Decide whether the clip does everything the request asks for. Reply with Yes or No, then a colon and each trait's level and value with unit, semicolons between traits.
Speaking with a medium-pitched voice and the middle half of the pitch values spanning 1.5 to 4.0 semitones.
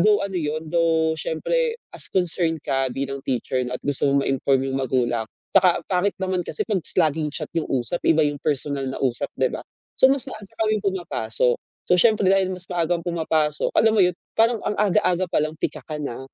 No: medium, 160 Hz; average, 5.3 semitones